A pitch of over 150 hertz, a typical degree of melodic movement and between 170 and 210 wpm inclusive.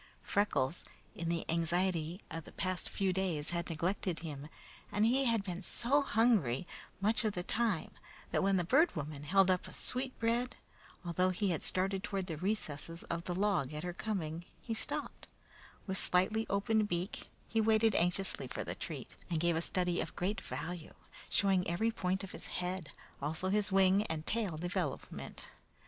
Yes: medium, 185 Hz; average, 3.6 semitones; average, 175 wpm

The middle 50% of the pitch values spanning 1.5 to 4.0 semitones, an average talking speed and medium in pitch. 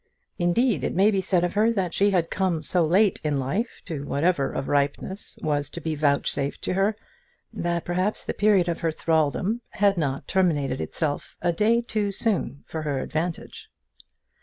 No: average, 4.7 semitones; average, 180 wpm; medium, 175 Hz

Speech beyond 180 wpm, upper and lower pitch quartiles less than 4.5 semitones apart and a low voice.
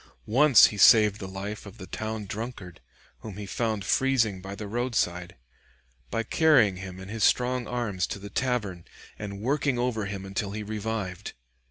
No: average, 170 wpm; average, 3.5 semitones; low, 105 Hz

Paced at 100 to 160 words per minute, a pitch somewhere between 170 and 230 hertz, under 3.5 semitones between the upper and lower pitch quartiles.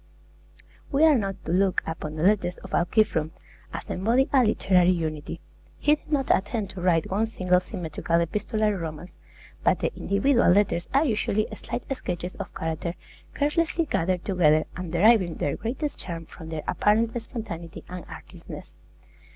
No: average, 155 wpm; high, 190 Hz; average, 5.0 semitones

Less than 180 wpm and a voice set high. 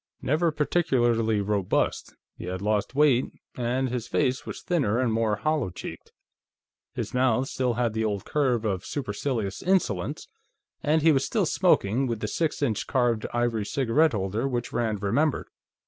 No: average, 160 wpm; low, 120 Hz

